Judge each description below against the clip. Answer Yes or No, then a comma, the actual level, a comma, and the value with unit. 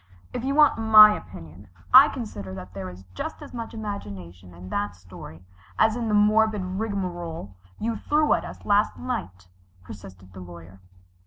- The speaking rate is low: No, average, 165 wpm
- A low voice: No, medium, 170 Hz